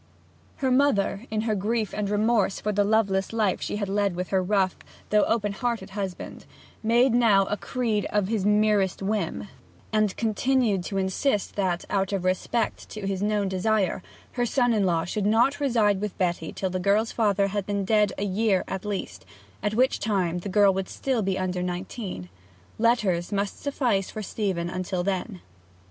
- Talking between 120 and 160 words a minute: No, average, 180 wpm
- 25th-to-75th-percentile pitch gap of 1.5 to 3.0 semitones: Yes, narrow, 2.5 semitones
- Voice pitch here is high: Yes, high, 205 Hz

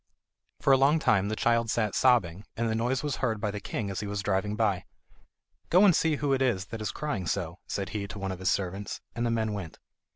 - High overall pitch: No, low, 110 Hz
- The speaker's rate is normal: No, fast, 250 wpm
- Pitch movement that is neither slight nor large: Yes, average, 3.7 semitones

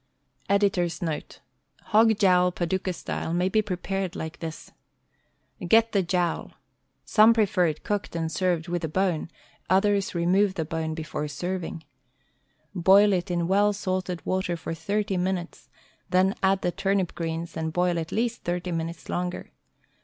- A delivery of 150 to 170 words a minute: Yes, average, 155 wpm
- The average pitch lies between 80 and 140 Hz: No, medium, 180 Hz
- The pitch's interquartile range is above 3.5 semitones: No, narrow, 2.6 semitones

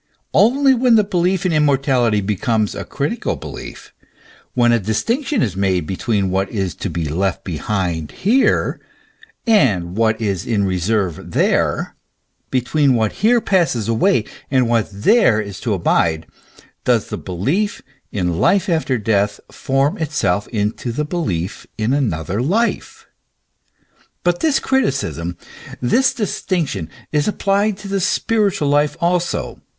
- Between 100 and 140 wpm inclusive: Yes, slow, 135 wpm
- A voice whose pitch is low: Yes, low, 120 Hz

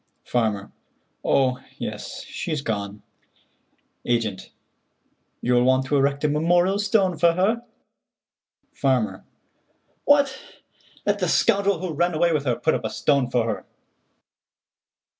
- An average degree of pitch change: No, wide, 6.2 semitones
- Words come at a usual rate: No, slow, 120 wpm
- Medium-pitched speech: Yes, medium, 145 Hz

